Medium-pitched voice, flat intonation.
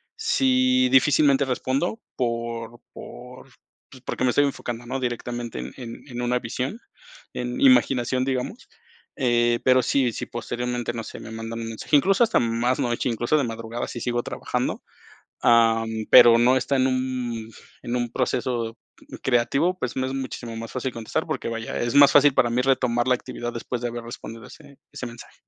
No: low, 125 Hz; narrow, 2.0 semitones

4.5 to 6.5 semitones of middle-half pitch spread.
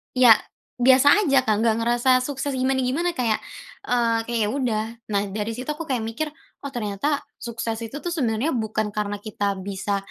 No: average, 3.5 semitones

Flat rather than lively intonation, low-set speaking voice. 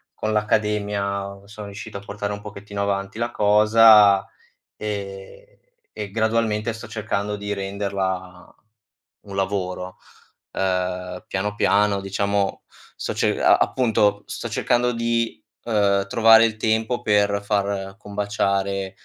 Yes: narrow, 1.6 semitones; low, 100 Hz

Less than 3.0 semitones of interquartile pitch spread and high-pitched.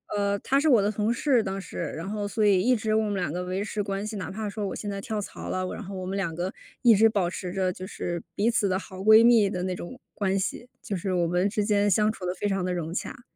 Yes: narrow, 2.6 semitones; high, 200 Hz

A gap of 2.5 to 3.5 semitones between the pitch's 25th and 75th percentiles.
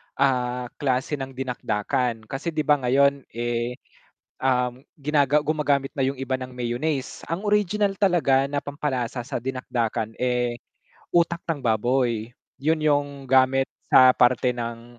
Yes: average, 2.8 semitones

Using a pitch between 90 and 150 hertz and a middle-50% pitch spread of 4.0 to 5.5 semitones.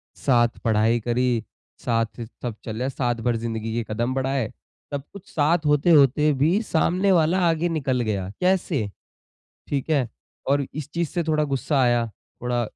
Yes: low, 135 Hz; average, 4.7 semitones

